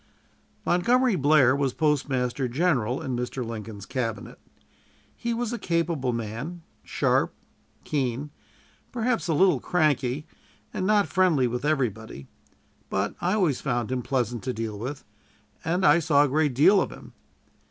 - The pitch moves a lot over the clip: Yes, wide, 6.0 semitones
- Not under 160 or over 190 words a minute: No, average, 140 wpm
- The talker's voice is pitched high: No, medium, 140 Hz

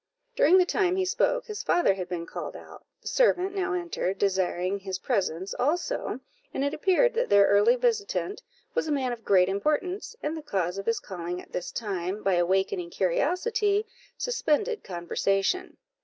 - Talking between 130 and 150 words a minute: No, average, 170 wpm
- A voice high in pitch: Yes, very high, 250 Hz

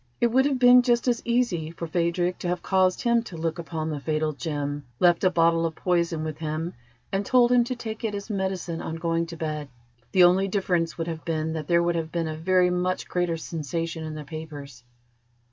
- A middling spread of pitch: Yes, average, 3.0 semitones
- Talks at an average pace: No, fast, 220 wpm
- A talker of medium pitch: Yes, medium, 170 Hz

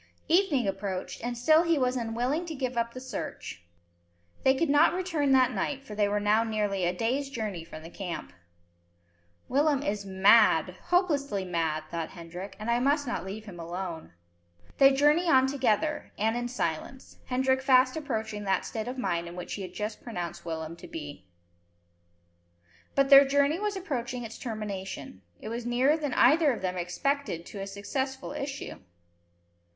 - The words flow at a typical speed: Yes, average, 170 wpm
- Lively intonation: Yes, wide, 6.3 semitones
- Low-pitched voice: No, high, 235 Hz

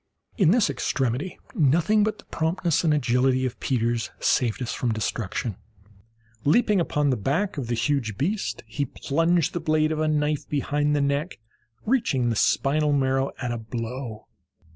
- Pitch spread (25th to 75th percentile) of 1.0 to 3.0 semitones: No, average, 4.5 semitones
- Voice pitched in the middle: Yes, medium, 145 Hz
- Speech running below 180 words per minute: Yes, average, 165 wpm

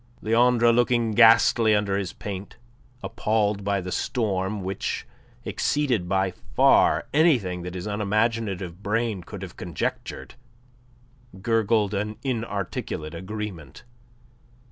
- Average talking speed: No, slow, 105 wpm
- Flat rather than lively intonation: No, average, 3.3 semitones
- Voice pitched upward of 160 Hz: No, low, 105 Hz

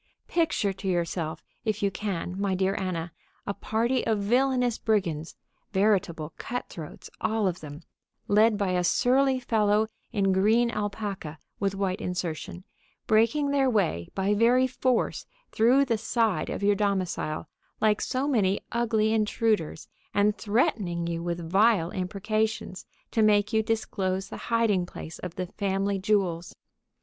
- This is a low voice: No, high, 205 Hz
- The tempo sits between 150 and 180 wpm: No, average, 140 wpm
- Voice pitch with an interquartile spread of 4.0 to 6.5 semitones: No, average, 3.5 semitones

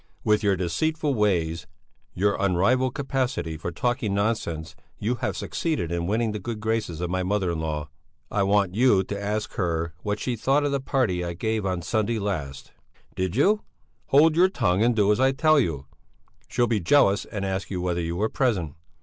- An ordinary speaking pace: Yes, average, 190 wpm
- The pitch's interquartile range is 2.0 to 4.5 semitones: No, wide, 5.5 semitones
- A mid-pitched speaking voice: No, low, 105 Hz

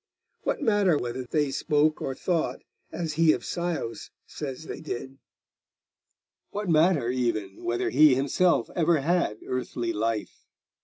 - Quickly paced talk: No, slow, 135 wpm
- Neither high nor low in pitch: Yes, medium, 145 Hz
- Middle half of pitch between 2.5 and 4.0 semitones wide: No, wide, 5.6 semitones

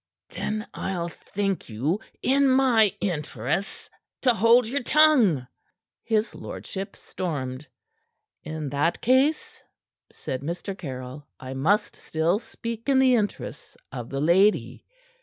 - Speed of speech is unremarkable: No, slow, 120 wpm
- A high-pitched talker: Yes, high, 195 Hz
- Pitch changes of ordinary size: No, wide, 7.9 semitones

